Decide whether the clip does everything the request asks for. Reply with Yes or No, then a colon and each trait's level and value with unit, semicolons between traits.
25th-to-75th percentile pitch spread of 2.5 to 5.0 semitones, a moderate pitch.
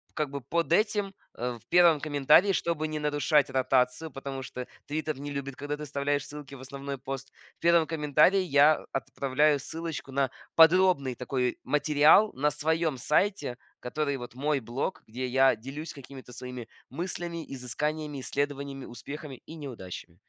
Yes: average, 2.8 semitones; medium, 145 Hz